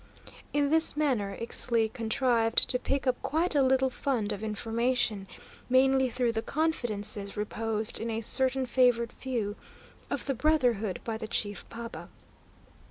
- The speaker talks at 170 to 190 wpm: No, average, 145 wpm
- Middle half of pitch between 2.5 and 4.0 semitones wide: Yes, average, 3.1 semitones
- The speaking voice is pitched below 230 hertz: No, high, 235 Hz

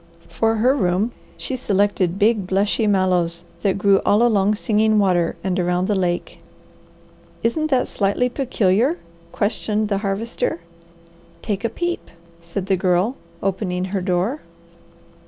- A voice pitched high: Yes, high, 200 Hz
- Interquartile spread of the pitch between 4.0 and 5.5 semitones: No, average, 3.3 semitones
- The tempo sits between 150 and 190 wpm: No, slow, 135 wpm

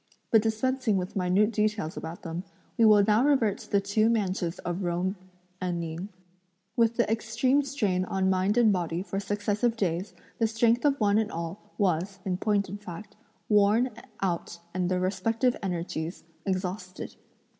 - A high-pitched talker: Yes, high, 200 Hz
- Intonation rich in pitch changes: No, average, 3.4 semitones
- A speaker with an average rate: Yes, average, 165 wpm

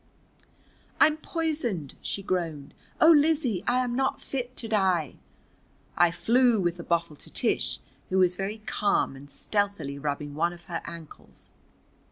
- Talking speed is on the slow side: No, average, 150 wpm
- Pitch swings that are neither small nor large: No, wide, 6.5 semitones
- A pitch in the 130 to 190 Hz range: Yes, medium, 185 Hz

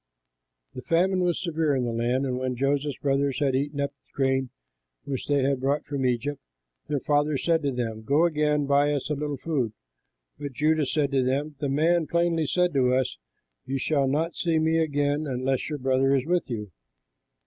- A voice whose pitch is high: No, medium, 140 Hz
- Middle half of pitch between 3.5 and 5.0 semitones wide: No, narrow, 2.5 semitones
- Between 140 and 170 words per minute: No, average, 195 wpm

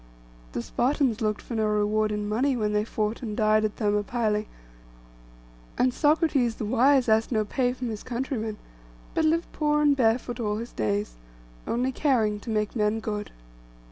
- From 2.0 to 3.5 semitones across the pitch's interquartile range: Yes, average, 3.2 semitones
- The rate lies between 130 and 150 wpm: No, average, 170 wpm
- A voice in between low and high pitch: No, high, 225 Hz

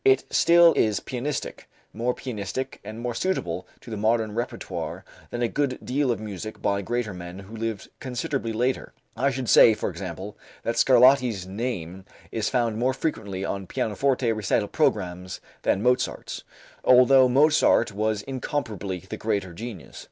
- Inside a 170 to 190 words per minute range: No, average, 150 wpm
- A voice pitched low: Yes, low, 115 Hz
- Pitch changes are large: No, average, 4.2 semitones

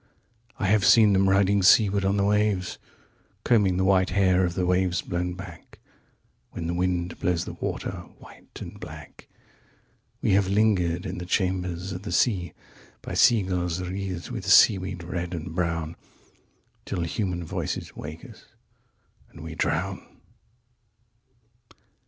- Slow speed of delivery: Yes, slow, 130 wpm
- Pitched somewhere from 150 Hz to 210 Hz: No, very low, 90 Hz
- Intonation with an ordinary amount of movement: No, narrow, 2.0 semitones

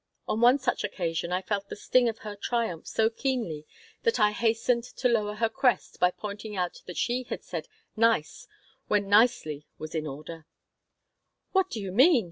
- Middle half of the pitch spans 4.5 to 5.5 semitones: Yes, average, 4.9 semitones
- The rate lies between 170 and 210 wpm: Yes, average, 180 wpm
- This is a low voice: No, high, 210 Hz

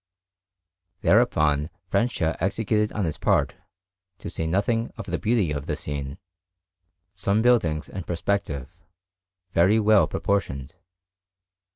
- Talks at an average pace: No, slow, 110 wpm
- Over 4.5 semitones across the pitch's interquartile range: Yes, wide, 5.6 semitones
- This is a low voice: Yes, very low, 95 Hz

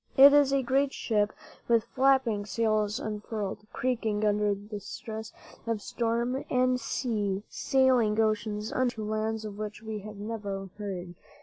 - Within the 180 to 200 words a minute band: No, average, 140 wpm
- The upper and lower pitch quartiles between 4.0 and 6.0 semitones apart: No, average, 2.8 semitones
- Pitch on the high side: Yes, high, 220 Hz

